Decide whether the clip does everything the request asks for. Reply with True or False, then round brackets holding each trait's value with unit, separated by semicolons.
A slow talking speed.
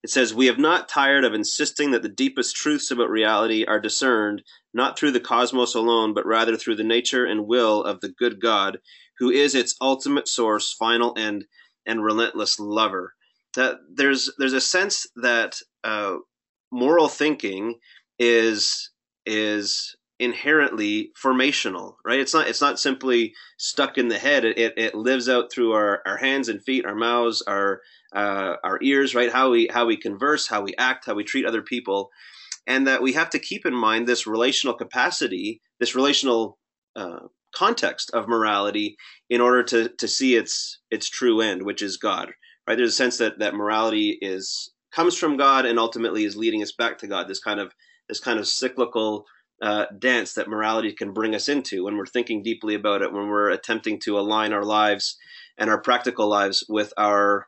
False (185 wpm)